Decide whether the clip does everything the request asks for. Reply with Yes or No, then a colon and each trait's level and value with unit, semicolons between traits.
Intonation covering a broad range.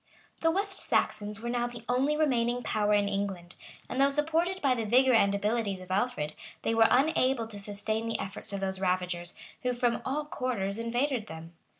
No: average, 4.4 semitones